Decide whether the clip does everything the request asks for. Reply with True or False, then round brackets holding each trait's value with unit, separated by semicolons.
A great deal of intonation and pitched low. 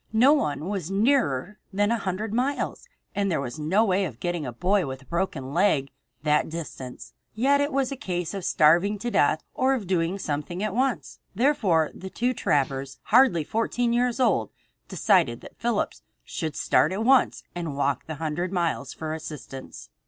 False (7.0 semitones; 185 Hz)